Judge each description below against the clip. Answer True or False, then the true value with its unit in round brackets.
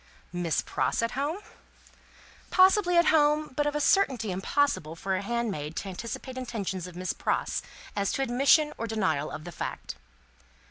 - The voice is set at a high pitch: True (230 Hz)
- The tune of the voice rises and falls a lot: True (8.0 semitones)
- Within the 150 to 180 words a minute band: True (155 wpm)